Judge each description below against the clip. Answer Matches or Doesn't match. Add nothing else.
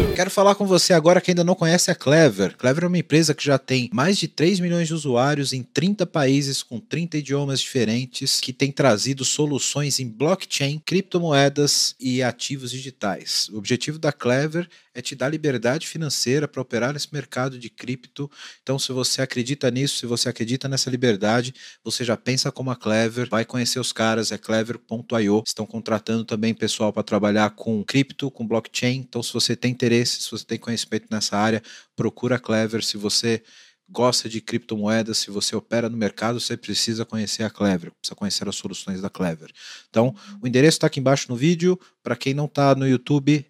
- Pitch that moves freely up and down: Doesn't match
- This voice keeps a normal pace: Doesn't match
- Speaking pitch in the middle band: Doesn't match